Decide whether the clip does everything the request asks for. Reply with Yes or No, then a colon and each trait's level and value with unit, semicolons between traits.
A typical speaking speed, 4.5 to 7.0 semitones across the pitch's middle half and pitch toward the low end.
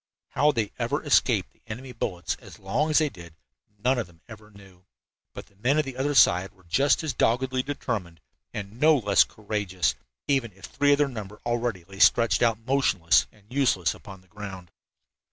Yes: average, 190 wpm; wide, 5.4 semitones; low, 110 Hz